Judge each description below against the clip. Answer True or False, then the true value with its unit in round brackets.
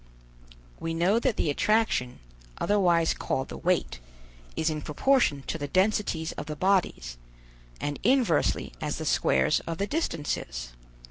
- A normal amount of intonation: False (5.9 semitones)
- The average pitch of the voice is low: False (165 Hz)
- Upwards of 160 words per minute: False (140 wpm)